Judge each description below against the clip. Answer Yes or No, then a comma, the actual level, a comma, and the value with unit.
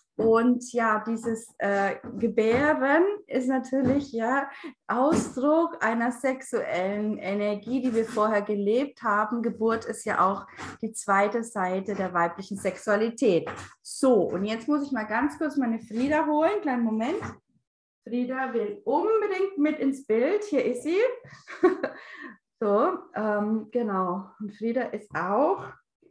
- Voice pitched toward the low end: No, high, 235 Hz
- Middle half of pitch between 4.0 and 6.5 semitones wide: Yes, average, 4.3 semitones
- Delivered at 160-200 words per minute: No, average, 130 wpm